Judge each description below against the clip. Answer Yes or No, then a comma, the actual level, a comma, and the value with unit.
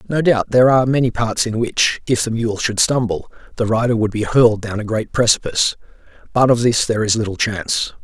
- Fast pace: Yes, fast, 215 wpm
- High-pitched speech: No, low, 115 Hz